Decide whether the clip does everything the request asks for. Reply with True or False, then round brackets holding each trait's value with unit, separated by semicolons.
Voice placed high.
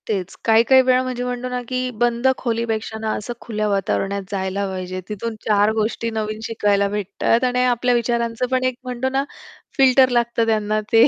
True (230 Hz)